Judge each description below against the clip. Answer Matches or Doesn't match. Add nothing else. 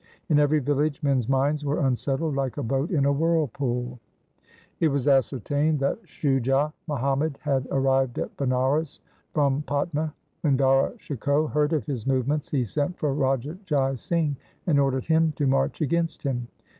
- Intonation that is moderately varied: Doesn't match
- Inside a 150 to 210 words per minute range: Matches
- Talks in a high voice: Doesn't match